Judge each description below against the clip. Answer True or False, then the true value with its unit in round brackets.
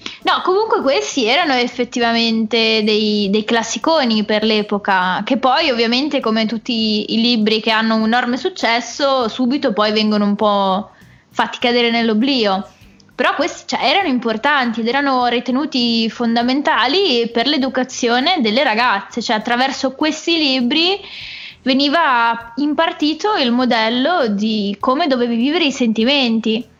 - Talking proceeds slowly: False (130 wpm)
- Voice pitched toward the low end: False (240 Hz)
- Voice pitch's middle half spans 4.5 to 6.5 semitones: False (3.3 semitones)